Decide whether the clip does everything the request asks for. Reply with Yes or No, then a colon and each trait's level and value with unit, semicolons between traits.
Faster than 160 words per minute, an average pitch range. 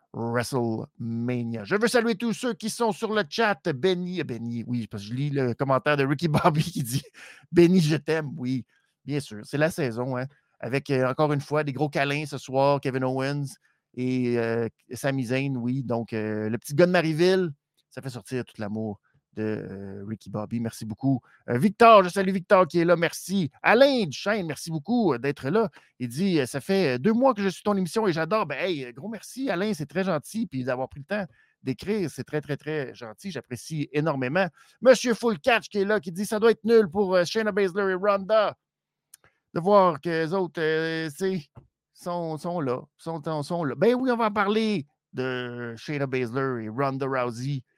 No: average, 200 wpm; wide, 7.1 semitones